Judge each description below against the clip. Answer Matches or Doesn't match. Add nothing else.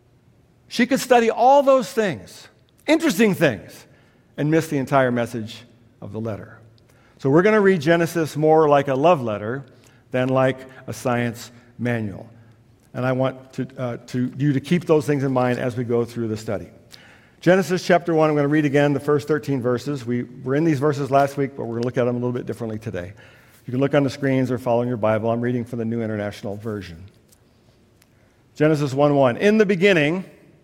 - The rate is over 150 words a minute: Matches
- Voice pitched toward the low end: Matches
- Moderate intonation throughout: Matches